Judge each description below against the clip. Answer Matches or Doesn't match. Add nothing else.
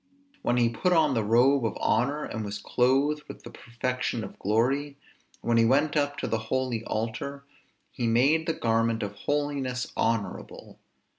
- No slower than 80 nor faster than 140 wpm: Doesn't match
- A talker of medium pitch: Doesn't match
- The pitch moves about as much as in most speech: Matches